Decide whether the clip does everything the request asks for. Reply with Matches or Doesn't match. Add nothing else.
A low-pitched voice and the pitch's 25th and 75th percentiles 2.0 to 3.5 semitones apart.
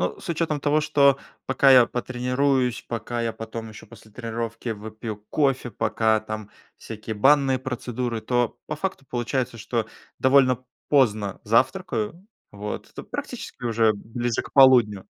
Matches